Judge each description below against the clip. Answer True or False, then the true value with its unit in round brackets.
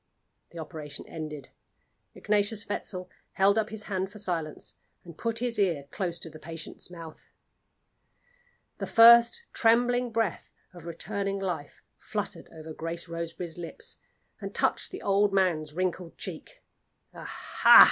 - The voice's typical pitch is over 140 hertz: True (185 Hz)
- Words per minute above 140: False (135 wpm)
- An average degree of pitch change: True (4.3 semitones)